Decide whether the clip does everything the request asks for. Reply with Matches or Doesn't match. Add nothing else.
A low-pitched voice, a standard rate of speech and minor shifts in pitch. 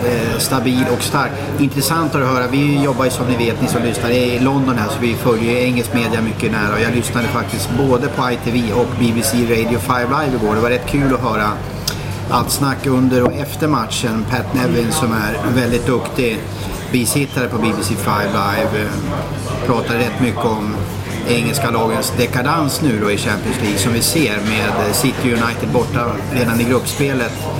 Matches